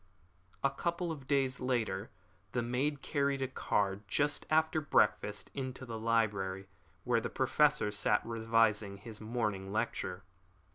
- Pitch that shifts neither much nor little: Yes, average, 4.7 semitones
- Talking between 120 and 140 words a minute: Yes, slow, 135 wpm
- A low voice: Yes, low, 115 Hz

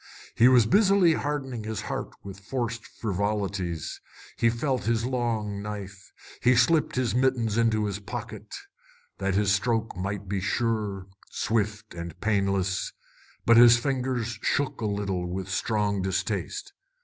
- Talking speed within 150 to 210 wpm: No, slow, 135 wpm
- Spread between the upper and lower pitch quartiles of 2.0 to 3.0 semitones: No, average, 3.5 semitones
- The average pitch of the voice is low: Yes, low, 110 Hz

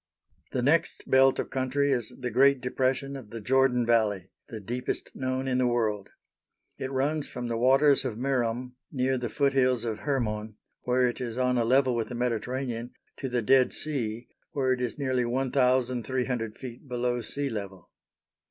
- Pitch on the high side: No, low, 125 Hz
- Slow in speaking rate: No, average, 170 wpm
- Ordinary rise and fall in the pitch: No, narrow, 2.0 semitones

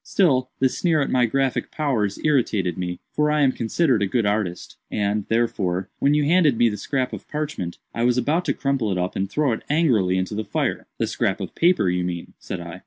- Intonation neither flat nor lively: No, wide, 6.8 semitones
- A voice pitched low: Yes, low, 120 Hz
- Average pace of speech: No, fast, 215 wpm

